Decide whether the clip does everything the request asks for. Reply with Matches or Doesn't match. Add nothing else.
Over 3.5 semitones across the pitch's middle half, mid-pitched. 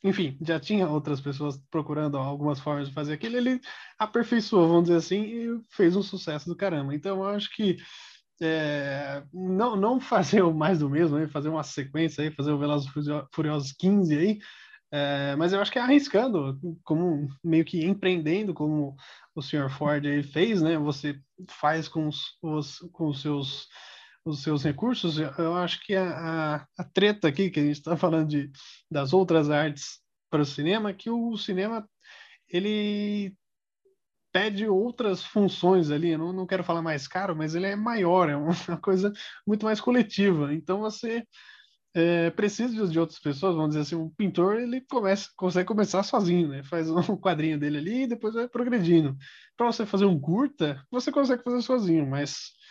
Matches